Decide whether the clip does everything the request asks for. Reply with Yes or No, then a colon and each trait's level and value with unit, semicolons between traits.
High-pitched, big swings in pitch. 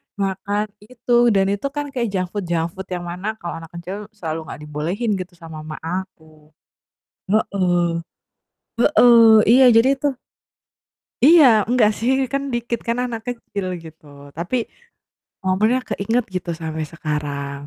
Yes: high, 195 Hz; wide, 5.8 semitones